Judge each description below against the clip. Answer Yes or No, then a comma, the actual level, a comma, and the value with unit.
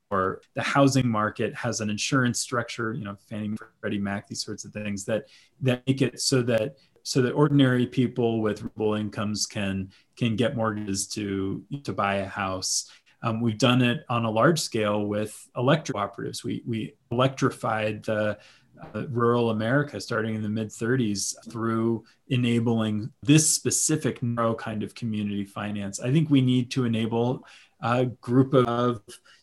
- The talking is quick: No, average, 165 wpm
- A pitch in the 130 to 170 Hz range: No, low, 115 Hz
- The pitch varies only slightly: No, average, 3.1 semitones